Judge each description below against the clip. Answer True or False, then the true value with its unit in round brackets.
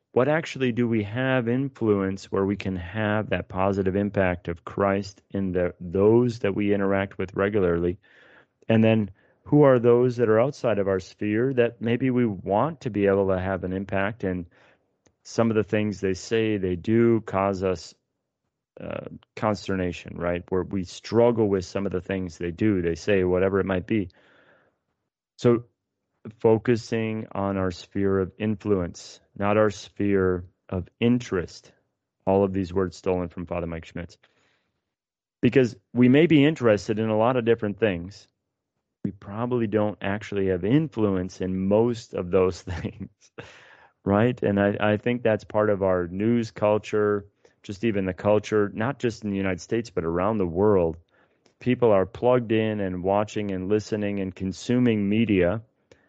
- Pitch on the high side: False (100 Hz)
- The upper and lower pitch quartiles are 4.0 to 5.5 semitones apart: False (3.2 semitones)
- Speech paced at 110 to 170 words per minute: True (165 wpm)